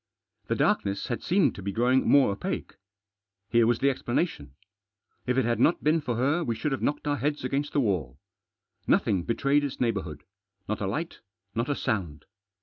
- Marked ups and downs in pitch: Yes, wide, 6.2 semitones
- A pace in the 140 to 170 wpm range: No, average, 185 wpm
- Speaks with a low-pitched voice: Yes, low, 120 Hz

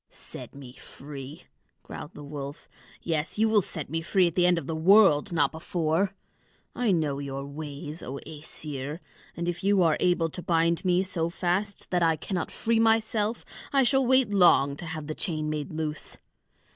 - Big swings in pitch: No, average, 4.1 semitones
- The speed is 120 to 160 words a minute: No, average, 185 wpm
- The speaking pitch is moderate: Yes, medium, 165 Hz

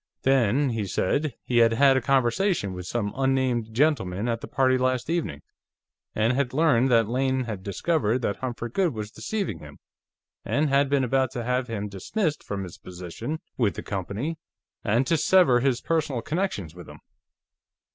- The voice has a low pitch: Yes, low, 125 Hz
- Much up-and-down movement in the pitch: No, average, 4.5 semitones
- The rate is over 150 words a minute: Yes, average, 175 wpm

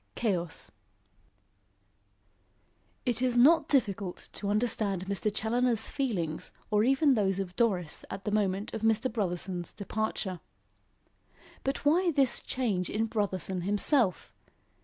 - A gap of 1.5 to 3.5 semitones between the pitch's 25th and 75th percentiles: No, average, 4.4 semitones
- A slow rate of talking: Yes, slow, 115 wpm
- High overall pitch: Yes, high, 210 Hz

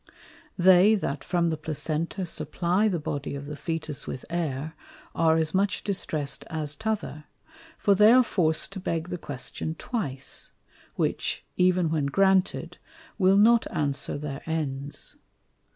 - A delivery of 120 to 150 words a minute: Yes, average, 140 wpm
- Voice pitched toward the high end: No, medium, 165 Hz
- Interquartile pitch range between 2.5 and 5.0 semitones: Yes, average, 4.1 semitones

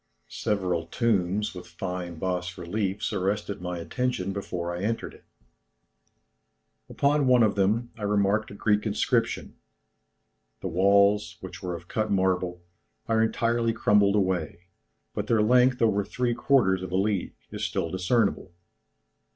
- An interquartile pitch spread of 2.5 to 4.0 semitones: Yes, average, 3.3 semitones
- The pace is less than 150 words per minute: Yes, average, 140 wpm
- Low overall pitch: Yes, low, 100 Hz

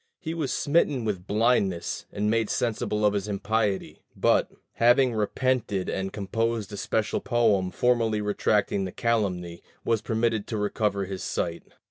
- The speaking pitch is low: Yes, low, 105 Hz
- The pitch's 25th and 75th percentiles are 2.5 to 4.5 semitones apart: Yes, average, 2.8 semitones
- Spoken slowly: No, average, 145 wpm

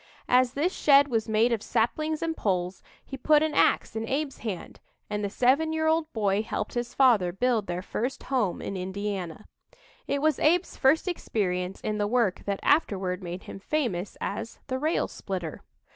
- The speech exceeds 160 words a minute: Yes, average, 180 wpm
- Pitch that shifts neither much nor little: No, wide, 6.4 semitones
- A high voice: Yes, high, 225 Hz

